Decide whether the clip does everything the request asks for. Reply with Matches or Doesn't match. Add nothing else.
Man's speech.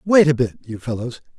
Matches